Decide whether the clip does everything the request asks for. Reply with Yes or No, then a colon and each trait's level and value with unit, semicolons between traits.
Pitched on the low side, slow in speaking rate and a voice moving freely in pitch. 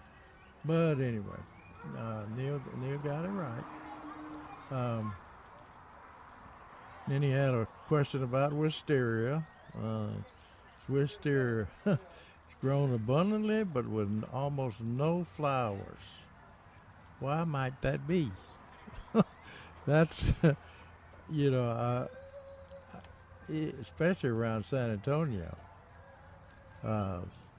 Yes: low, 120 Hz; slow, 85 wpm; wide, 6.6 semitones